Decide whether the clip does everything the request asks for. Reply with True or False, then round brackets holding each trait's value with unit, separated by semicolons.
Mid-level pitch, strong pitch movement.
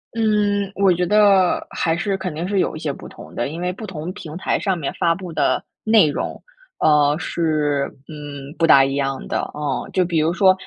False (170 Hz; 4.3 semitones)